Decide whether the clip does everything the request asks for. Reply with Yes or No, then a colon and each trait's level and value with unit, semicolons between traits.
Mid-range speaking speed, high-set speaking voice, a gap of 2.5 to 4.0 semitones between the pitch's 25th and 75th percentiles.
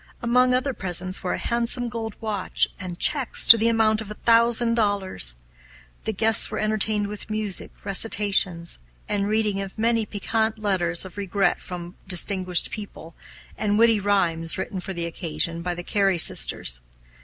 Yes: average, 160 wpm; high, 205 Hz; average, 3.3 semitones